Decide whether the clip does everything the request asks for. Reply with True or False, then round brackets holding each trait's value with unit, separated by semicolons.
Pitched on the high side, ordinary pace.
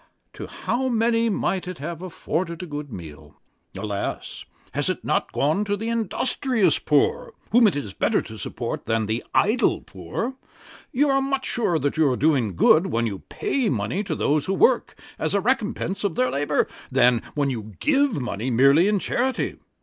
False (170 Hz; 180 wpm)